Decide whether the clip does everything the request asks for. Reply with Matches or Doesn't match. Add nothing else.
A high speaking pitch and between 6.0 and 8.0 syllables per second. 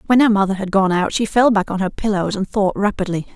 Matches